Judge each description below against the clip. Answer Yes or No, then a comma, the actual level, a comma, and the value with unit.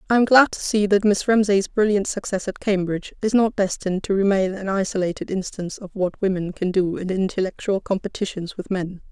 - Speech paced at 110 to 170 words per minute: No, average, 195 wpm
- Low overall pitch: No, high, 195 Hz